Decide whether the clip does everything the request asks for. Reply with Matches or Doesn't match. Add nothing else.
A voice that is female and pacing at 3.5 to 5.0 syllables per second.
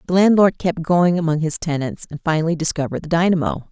Doesn't match